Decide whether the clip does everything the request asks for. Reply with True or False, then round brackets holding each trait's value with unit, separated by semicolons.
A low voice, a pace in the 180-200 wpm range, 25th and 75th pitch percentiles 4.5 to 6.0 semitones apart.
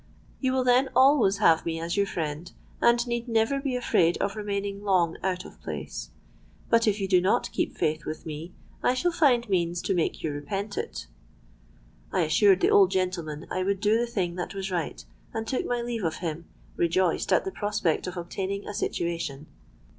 False (190 Hz; 190 wpm; 4.9 semitones)